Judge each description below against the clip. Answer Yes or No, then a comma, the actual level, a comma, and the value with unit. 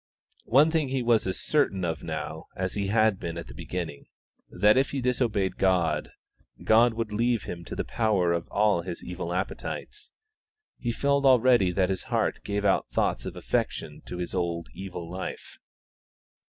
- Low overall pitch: Yes, low, 100 Hz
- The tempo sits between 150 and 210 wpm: Yes, average, 175 wpm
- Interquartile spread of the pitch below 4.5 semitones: No, average, 5.1 semitones